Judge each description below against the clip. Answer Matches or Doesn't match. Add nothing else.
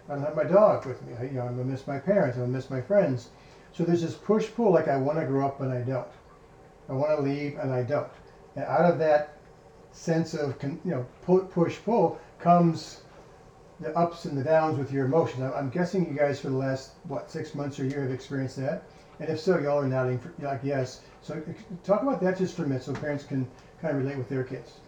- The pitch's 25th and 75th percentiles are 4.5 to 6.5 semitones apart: Doesn't match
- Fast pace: Matches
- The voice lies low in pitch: Doesn't match